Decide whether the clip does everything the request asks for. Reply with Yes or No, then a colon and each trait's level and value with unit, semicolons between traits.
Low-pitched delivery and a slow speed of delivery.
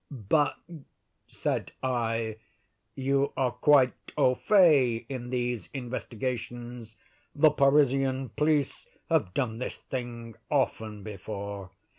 Yes: low, 125 Hz; slow, 100 wpm